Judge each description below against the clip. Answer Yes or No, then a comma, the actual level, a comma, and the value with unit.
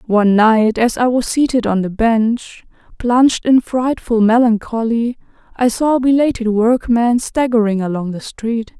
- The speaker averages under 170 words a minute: Yes, average, 150 wpm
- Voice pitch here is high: Yes, high, 230 Hz